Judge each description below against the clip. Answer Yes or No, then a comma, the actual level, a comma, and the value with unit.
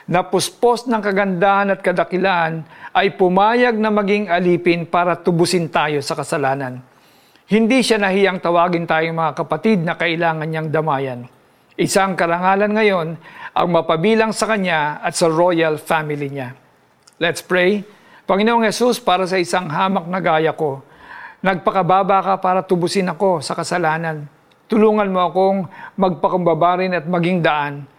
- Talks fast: No, average, 135 wpm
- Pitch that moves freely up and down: No, average, 3.2 semitones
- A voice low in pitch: No, medium, 180 Hz